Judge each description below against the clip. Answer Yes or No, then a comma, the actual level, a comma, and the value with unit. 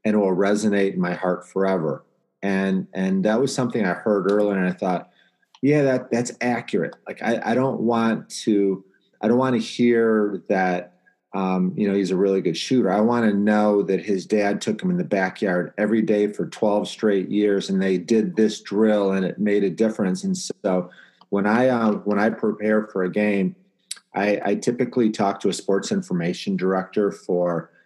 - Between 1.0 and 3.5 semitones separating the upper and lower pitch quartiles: Yes, average, 2.8 semitones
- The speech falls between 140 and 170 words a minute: No, average, 200 wpm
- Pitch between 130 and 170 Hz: No, low, 105 Hz